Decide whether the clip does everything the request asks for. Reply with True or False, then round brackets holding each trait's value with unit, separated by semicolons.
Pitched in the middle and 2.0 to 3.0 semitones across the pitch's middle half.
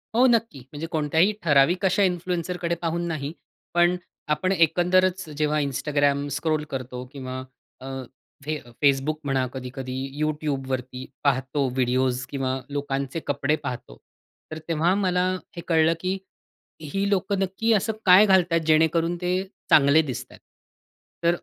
False (155 Hz; 4.6 semitones)